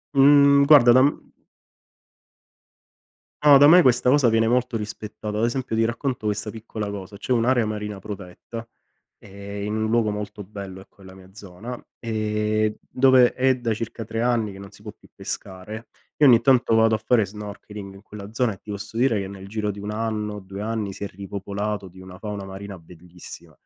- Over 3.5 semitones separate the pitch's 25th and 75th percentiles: No, narrow, 2.6 semitones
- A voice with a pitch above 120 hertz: No, low, 105 Hz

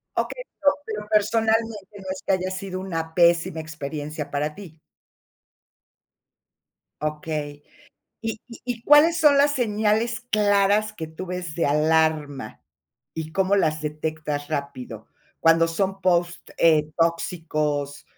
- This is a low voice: No, medium, 170 Hz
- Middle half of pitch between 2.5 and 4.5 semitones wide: No, average, 5.3 semitones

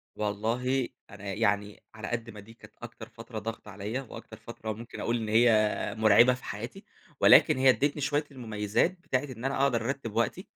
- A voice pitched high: No, low, 115 Hz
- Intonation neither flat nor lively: Yes, average, 3.1 semitones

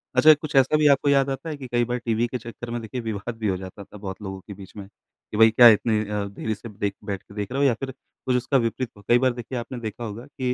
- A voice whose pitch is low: Yes, low, 120 Hz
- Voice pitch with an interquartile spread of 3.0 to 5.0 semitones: Yes, average, 3.8 semitones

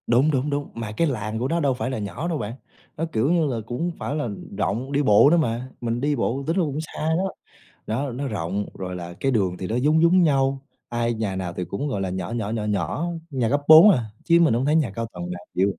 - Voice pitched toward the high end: No, low, 125 Hz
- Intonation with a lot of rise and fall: Yes, wide, 5.9 semitones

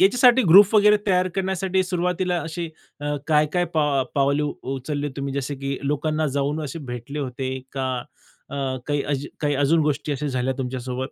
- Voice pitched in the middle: Yes, medium, 150 Hz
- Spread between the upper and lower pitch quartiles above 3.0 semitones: Yes, average, 4.4 semitones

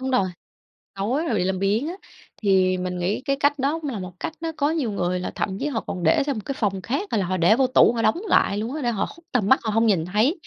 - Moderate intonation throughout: No, wide, 6.5 semitones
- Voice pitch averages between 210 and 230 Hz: Yes, high, 220 Hz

